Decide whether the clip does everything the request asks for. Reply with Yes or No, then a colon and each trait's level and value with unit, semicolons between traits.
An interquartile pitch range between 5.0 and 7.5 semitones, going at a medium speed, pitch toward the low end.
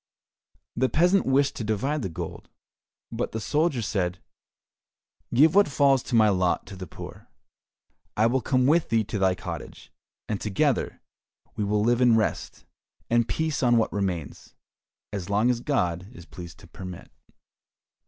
Yes: wide, 5.4 semitones; average, 160 wpm; low, 115 Hz